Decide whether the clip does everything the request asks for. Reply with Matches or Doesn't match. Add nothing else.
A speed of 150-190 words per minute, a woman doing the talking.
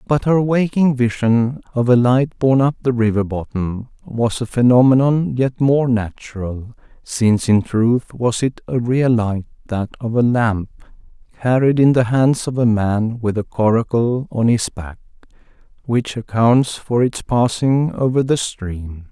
Doesn't match